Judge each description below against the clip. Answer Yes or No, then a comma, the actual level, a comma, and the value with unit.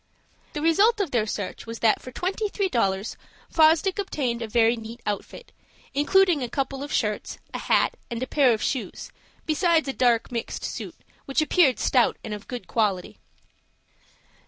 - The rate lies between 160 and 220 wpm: Yes, average, 170 wpm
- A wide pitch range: Yes, wide, 5.9 semitones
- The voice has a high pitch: Yes, very high, 255 Hz